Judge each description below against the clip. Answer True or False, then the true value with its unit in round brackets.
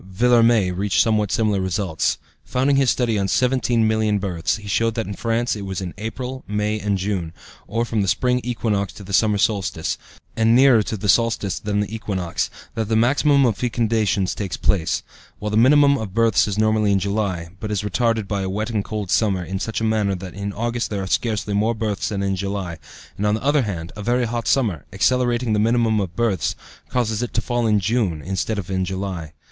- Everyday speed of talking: False (210 wpm)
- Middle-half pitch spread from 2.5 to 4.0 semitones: True (2.9 semitones)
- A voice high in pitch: False (105 Hz)